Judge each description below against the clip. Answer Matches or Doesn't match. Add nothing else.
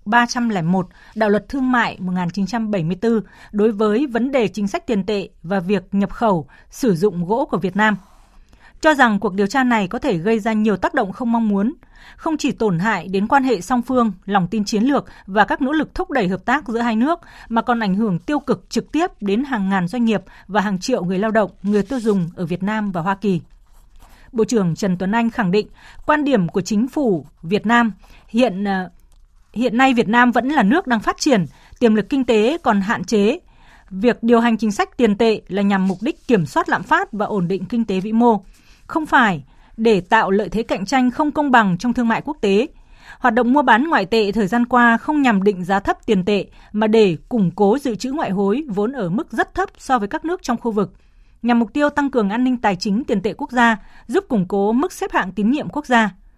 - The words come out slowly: Doesn't match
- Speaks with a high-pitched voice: Matches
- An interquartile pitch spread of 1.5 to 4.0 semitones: Matches